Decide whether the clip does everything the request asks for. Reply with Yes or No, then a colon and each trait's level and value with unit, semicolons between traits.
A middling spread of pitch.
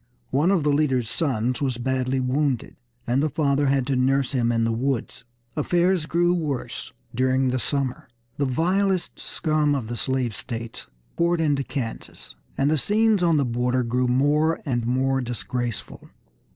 Yes: average, 3.5 semitones